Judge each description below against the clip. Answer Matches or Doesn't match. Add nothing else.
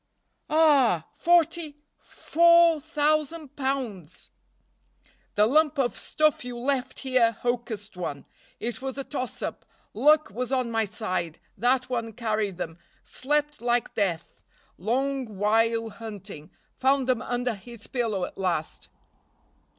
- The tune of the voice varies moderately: Matches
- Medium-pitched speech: Doesn't match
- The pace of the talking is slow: Matches